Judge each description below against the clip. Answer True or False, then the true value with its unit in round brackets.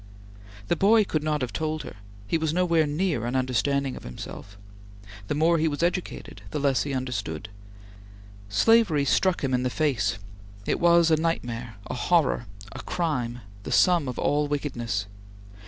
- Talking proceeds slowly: False (165 wpm)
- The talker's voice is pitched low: False (145 Hz)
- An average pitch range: True (5.0 semitones)